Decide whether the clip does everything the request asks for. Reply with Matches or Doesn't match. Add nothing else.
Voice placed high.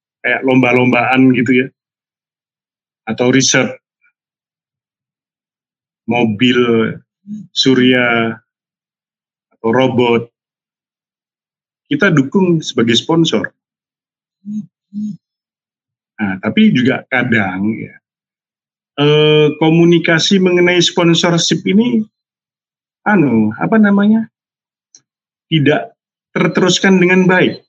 Doesn't match